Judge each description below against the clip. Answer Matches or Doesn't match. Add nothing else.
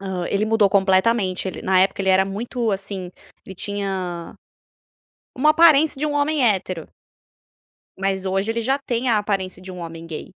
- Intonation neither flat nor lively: Matches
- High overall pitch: Matches